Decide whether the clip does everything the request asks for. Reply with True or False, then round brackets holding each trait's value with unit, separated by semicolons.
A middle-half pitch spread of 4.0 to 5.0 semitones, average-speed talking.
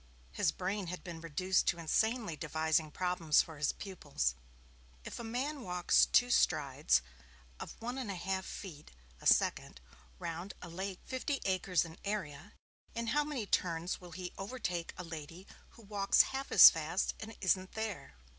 True (4.4 semitones; 165 wpm)